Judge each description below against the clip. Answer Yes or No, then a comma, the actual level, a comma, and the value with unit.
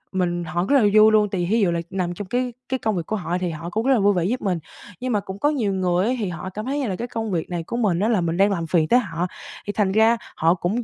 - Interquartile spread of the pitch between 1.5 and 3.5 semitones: No, average, 4.1 semitones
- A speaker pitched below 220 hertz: Yes, high, 195 Hz